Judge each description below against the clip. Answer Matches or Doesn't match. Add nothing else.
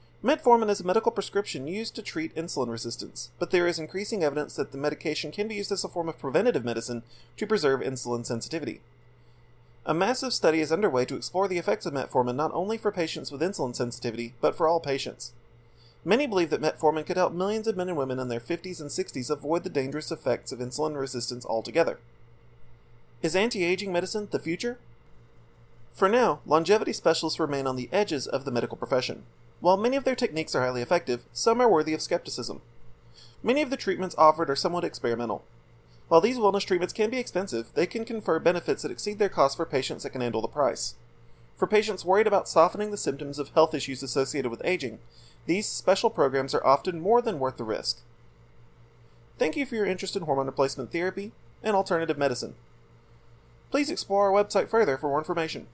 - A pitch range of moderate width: Doesn't match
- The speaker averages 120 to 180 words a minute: Doesn't match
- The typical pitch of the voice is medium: Matches